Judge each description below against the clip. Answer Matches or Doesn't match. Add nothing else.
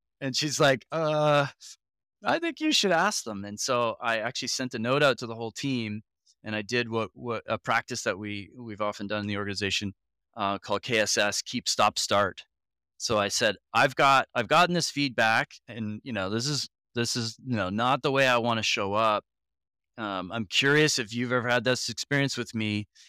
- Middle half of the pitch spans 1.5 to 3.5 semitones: Doesn't match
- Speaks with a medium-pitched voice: Doesn't match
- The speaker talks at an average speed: Doesn't match